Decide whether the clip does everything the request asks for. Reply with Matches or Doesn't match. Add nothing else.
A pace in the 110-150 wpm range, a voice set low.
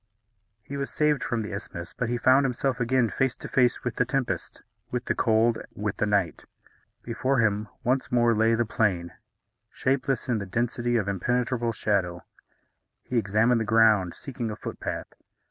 Doesn't match